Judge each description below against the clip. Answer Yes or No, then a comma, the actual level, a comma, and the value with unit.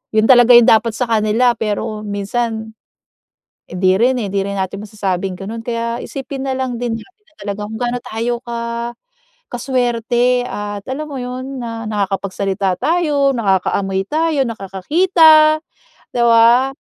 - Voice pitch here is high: Yes, high, 235 Hz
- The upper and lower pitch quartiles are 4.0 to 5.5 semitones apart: No, average, 3.6 semitones